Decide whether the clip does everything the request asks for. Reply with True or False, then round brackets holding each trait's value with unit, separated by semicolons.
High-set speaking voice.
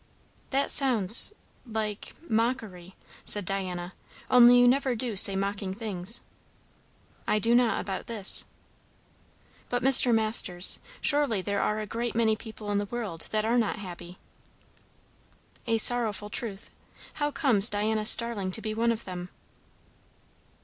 True (220 Hz)